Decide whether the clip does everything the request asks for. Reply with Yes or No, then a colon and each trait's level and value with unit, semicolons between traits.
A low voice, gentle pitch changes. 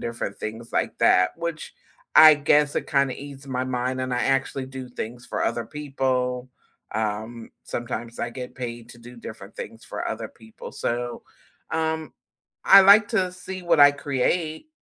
No: low, 130 Hz; average, 4.0 semitones